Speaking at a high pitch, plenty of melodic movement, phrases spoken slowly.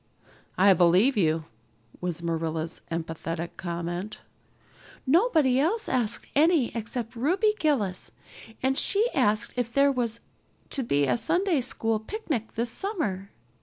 Yes: high, 230 Hz; wide, 8.4 semitones; slow, 125 wpm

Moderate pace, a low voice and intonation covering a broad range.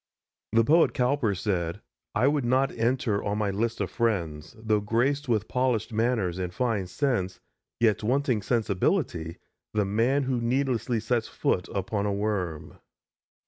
No: average, 145 wpm; low, 110 Hz; average, 3.9 semitones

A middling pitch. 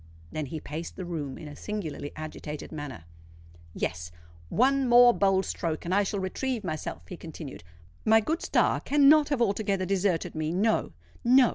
Yes: medium, 180 Hz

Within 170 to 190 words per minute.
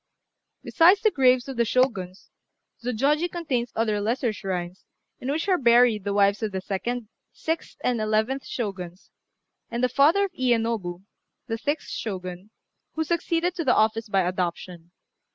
No: average, 155 wpm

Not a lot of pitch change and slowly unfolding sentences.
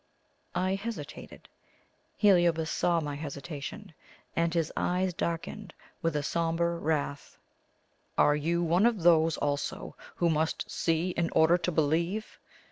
Yes: narrow, 1.9 semitones; slow, 125 wpm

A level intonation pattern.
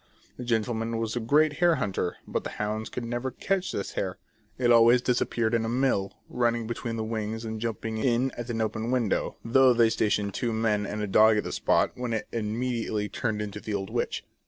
Yes: narrow, 2.0 semitones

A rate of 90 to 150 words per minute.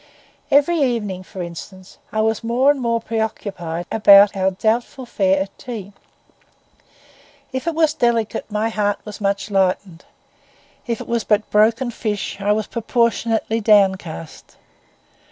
Yes: slow, 135 wpm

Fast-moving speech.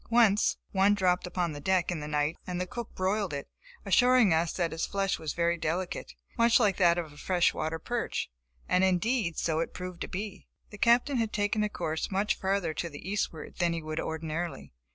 Yes: fast, 210 wpm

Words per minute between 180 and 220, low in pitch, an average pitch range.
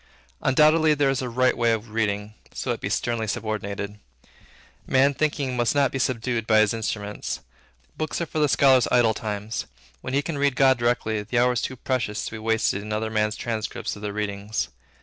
Yes: average, 200 wpm; low, 115 Hz; average, 3.6 semitones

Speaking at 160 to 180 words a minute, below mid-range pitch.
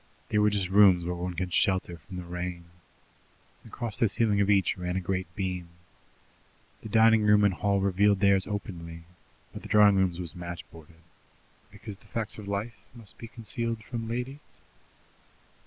Yes: average, 170 wpm; low, 100 Hz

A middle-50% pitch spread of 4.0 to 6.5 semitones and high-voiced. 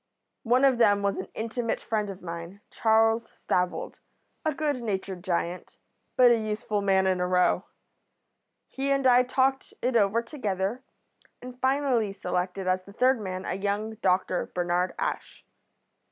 Yes: average, 5.0 semitones; high, 210 Hz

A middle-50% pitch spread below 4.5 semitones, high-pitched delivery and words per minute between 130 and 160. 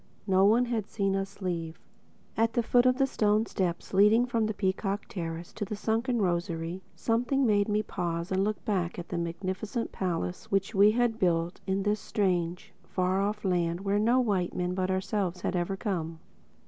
No: average, 3.4 semitones; high, 195 Hz; average, 185 wpm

